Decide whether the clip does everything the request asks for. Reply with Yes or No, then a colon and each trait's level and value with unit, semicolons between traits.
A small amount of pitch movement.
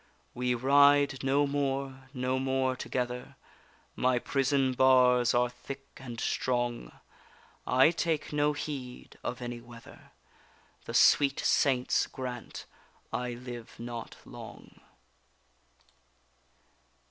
Yes: narrow, 2.0 semitones